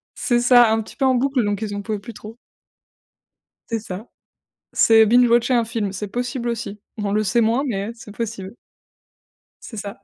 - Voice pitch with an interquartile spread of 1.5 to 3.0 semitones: Yes, average, 2.7 semitones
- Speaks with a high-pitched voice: Yes, high, 225 Hz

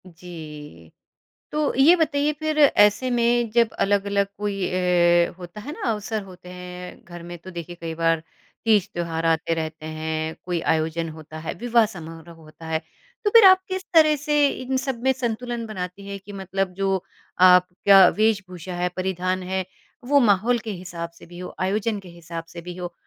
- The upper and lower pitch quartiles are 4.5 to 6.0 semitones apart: Yes, average, 4.8 semitones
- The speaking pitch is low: No, medium, 185 Hz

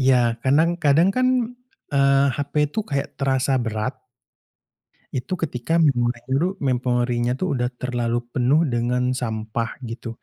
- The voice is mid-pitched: No, low, 130 Hz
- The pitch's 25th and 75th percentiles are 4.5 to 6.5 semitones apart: No, narrow, 2.6 semitones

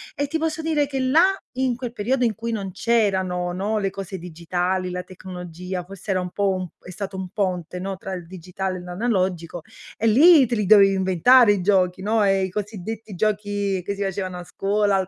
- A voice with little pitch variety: No, average, 3.1 semitones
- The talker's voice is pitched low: No, high, 195 Hz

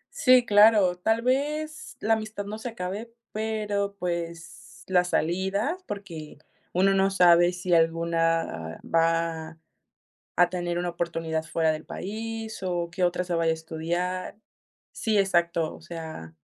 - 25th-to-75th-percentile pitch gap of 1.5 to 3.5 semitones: No, average, 3.9 semitones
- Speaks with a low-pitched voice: No, medium, 180 Hz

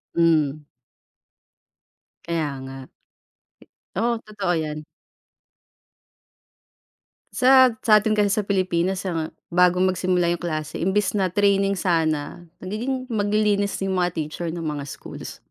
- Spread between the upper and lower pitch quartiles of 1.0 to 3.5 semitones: No, average, 4.1 semitones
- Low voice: No, medium, 185 Hz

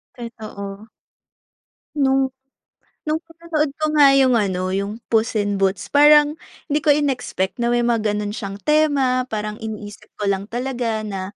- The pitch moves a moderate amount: No, wide, 5.7 semitones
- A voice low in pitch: No, high, 235 Hz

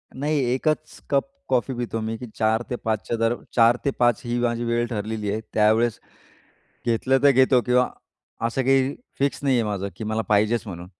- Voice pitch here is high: No, low, 120 Hz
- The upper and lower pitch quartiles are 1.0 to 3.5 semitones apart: Yes, average, 2.8 semitones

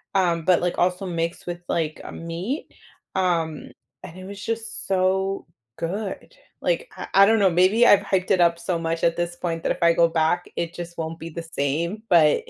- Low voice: No, medium, 175 Hz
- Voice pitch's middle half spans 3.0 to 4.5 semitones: No, narrow, 2.5 semitones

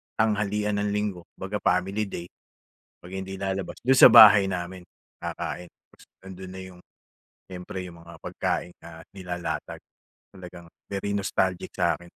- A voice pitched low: Yes, very low, 95 Hz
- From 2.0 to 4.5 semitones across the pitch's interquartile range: Yes, narrow, 2.4 semitones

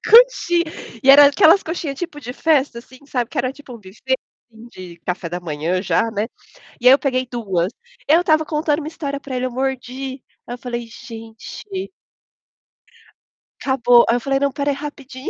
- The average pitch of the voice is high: Yes, very high, 260 Hz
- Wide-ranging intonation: No, average, 3.7 semitones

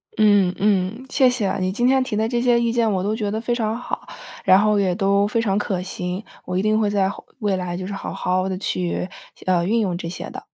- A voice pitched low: No, high, 205 Hz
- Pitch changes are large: No, average, 3.2 semitones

